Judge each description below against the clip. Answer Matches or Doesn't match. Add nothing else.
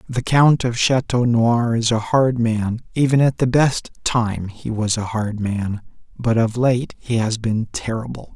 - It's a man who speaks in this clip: Matches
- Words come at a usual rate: Matches